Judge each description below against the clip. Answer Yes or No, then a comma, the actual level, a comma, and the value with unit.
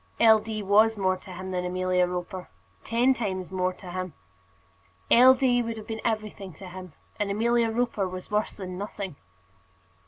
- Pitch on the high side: Yes, high, 200 Hz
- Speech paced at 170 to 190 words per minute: Yes, average, 175 wpm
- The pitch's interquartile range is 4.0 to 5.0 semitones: No, average, 3.3 semitones